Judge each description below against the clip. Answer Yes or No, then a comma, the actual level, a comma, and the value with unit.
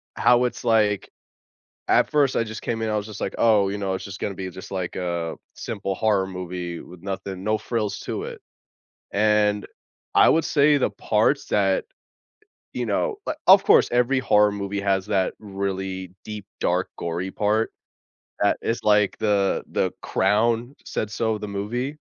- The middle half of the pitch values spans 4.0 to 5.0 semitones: No, average, 2.7 semitones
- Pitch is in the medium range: No, low, 105 Hz